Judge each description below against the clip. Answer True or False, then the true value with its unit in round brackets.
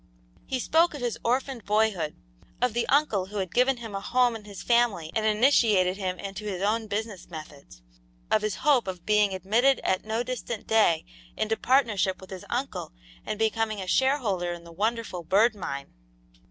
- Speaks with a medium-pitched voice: False (215 Hz)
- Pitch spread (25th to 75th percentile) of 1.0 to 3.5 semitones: False (4.1 semitones)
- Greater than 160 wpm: True (180 wpm)